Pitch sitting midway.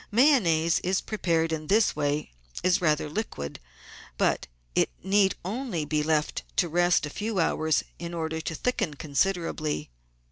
Yes: medium, 165 Hz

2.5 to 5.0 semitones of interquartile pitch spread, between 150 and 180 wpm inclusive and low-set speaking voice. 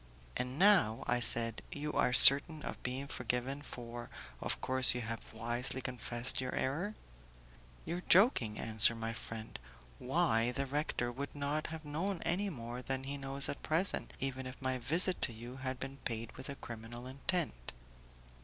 Yes: average, 3.5 semitones; average, 175 wpm; low, 130 Hz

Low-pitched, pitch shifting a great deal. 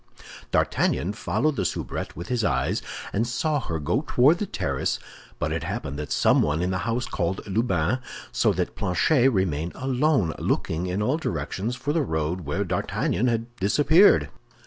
Yes: low, 100 Hz; wide, 7.0 semitones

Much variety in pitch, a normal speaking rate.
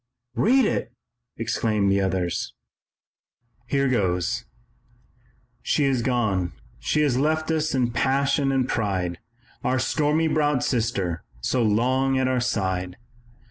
No: wide, 5.8 semitones; slow, 125 wpm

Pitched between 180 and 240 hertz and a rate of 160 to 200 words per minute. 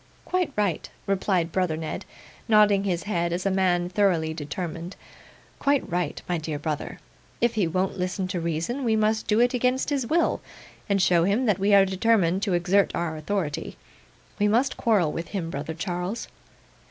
Yes: high, 190 Hz; average, 175 wpm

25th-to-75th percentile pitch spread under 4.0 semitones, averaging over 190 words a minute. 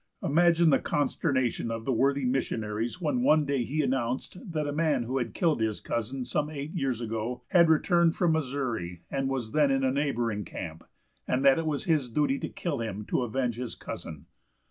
No: average, 4.4 semitones; average, 200 wpm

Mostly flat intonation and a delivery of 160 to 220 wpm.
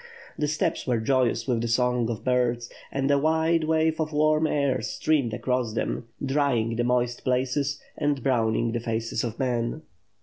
No: average, 3.7 semitones; average, 170 wpm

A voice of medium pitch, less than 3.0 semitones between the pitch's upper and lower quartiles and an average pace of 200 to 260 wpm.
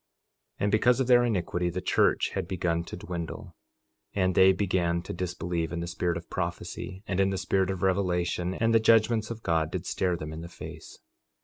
No: very low, 90 Hz; narrow, 2.5 semitones; fast, 205 wpm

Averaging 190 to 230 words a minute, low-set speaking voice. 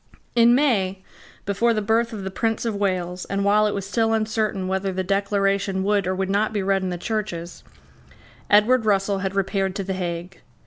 No: average, 195 wpm; high, 200 Hz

